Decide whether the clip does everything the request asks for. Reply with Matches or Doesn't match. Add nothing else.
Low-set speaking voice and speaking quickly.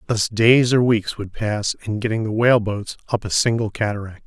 Matches